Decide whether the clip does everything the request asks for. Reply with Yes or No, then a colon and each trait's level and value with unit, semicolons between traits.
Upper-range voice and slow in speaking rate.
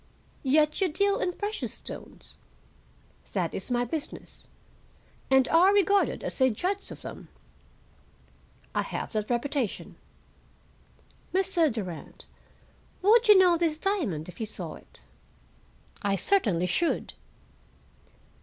Yes: very high, 305 Hz; slow, 115 wpm